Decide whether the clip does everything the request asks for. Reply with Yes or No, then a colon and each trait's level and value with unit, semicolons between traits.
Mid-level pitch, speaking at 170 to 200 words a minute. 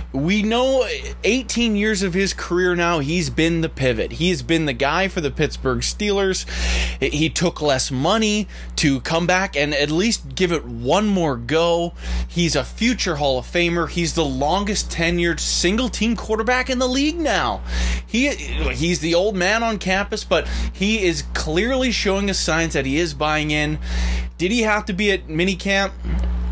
Yes: medium, 170 Hz; average, 180 wpm